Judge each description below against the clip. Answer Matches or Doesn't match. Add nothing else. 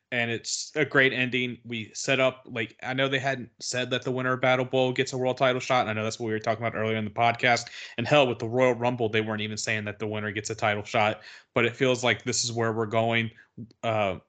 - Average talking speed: Doesn't match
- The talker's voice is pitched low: Matches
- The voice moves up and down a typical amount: Doesn't match